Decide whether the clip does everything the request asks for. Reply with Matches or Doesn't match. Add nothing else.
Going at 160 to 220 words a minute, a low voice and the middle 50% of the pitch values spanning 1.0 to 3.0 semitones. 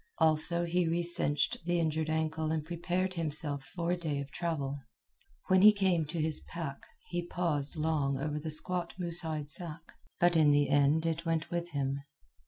Doesn't match